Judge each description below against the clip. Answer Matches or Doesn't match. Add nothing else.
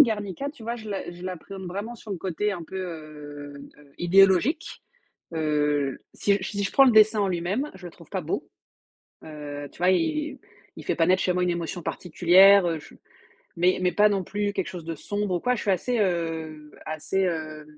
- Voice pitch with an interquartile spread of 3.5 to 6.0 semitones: Matches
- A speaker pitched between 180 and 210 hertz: Matches